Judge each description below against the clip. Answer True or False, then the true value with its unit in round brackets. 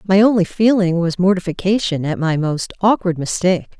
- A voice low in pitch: False (185 Hz)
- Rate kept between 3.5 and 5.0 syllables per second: False (5.3 syllables/s)